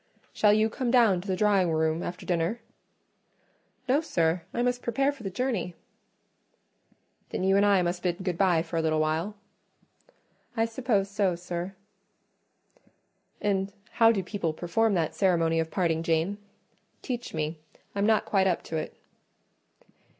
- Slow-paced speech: No, average, 155 wpm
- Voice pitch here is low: No, high, 190 Hz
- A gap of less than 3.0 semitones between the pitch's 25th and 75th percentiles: No, average, 4.2 semitones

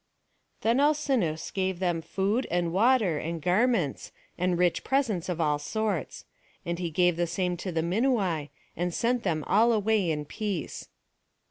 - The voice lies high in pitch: No, medium, 180 Hz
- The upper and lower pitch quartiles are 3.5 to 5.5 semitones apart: Yes, average, 4.7 semitones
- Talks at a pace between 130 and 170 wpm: Yes, average, 155 wpm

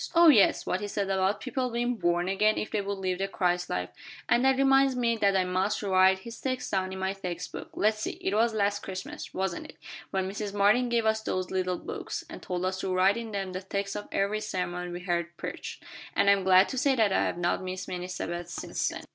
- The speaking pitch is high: Yes, high, 195 Hz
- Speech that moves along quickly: Yes, fast, 245 wpm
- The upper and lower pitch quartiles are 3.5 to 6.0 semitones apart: No, average, 2.8 semitones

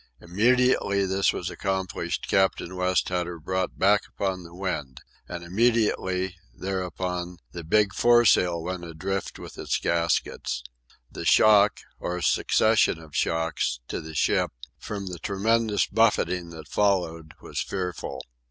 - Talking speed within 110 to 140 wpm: Yes, slow, 135 wpm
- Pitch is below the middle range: Yes, very low, 95 Hz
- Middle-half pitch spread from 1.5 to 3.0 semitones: Yes, narrow, 2.6 semitones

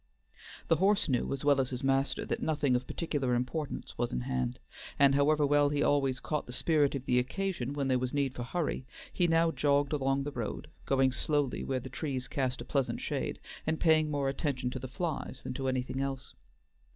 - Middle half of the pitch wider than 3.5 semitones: No, narrow, 2.4 semitones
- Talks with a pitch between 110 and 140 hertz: Yes, low, 135 Hz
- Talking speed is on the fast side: Yes, fast, 210 wpm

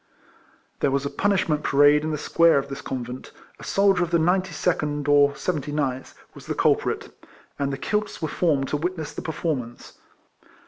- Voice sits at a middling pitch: Yes, medium, 150 Hz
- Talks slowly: No, average, 185 wpm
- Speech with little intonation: No, average, 3.3 semitones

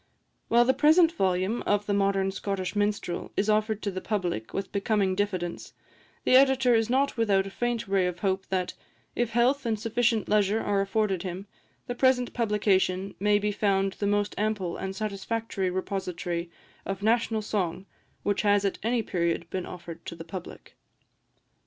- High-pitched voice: Yes, high, 205 Hz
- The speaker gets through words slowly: No, average, 170 wpm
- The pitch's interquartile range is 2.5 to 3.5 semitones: Yes, average, 2.9 semitones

